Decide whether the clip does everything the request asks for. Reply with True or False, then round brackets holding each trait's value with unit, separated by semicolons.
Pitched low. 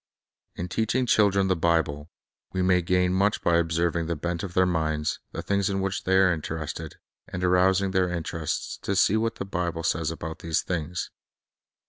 True (90 Hz)